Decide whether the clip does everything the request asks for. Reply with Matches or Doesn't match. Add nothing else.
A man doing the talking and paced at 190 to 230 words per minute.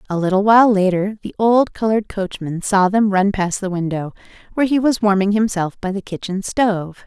Doesn't match